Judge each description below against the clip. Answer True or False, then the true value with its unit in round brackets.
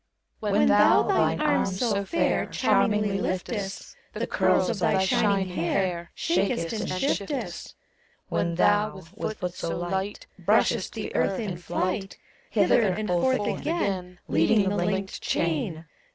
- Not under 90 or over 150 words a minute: True (140 wpm)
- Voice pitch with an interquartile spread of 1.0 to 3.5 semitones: True (2.7 semitones)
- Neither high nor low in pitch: False (195 Hz)